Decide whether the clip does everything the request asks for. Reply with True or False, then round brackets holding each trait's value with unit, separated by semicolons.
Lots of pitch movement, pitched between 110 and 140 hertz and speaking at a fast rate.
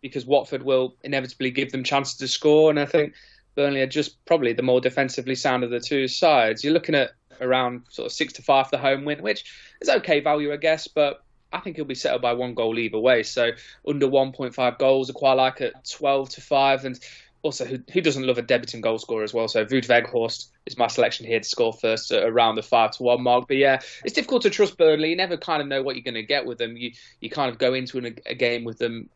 False (2.9 semitones; 135 Hz; 255 wpm)